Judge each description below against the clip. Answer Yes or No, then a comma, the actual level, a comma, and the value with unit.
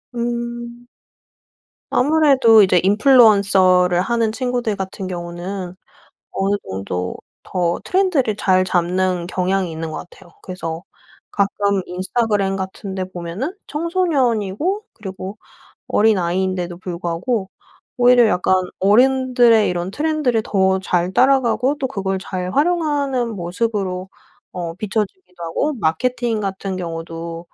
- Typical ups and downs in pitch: Yes, average, 5.0 semitones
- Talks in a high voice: Yes, high, 195 Hz